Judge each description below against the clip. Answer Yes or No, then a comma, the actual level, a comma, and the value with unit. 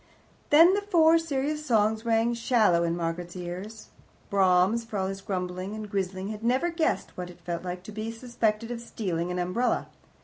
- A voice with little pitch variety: No, average, 4.7 semitones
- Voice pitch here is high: Yes, high, 215 Hz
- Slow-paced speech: No, average, 180 wpm